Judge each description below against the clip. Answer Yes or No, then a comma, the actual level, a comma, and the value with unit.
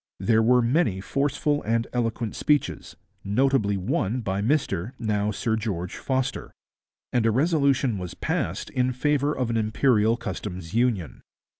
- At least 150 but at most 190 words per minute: No, average, 140 wpm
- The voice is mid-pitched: No, low, 115 Hz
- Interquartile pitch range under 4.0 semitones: No, average, 4.3 semitones